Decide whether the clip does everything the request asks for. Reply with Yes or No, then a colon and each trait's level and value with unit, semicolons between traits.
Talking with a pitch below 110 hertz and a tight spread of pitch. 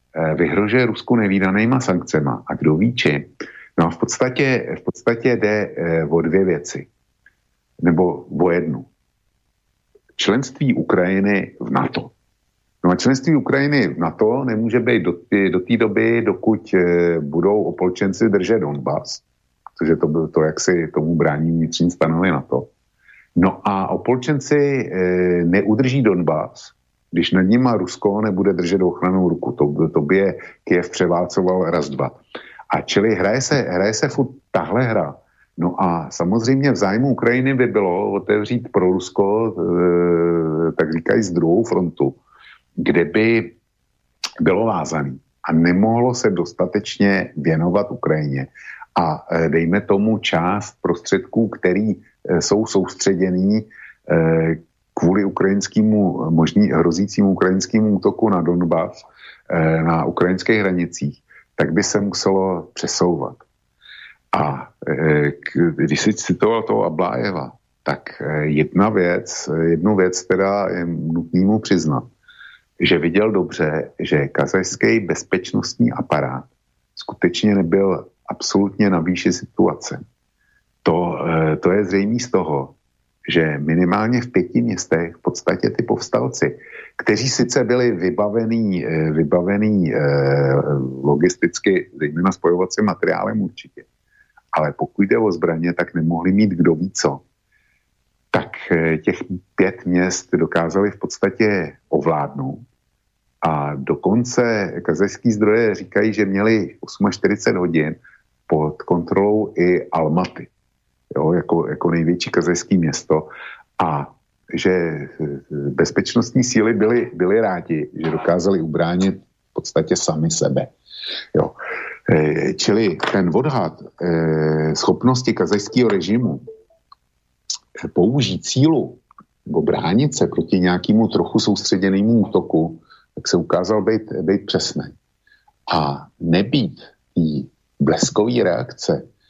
No: very low, 90 Hz; average, 4.7 semitones